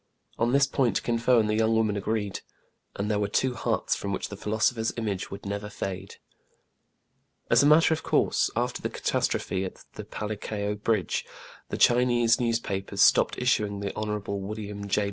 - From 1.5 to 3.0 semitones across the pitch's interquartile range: Yes, narrow, 2.5 semitones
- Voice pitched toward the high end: No, low, 105 Hz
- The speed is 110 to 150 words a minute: No, average, 175 wpm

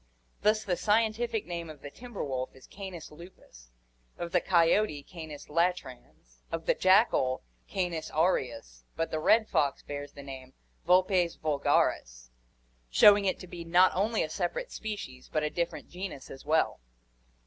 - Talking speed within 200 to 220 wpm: No, average, 155 wpm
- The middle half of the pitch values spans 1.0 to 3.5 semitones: No, average, 4.9 semitones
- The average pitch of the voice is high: No, medium, 170 Hz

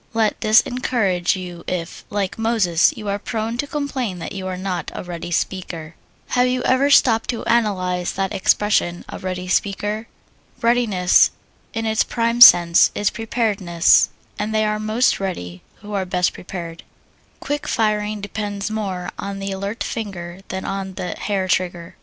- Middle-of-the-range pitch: No, high, 200 Hz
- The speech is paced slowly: No, average, 160 wpm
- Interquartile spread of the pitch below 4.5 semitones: Yes, average, 3.5 semitones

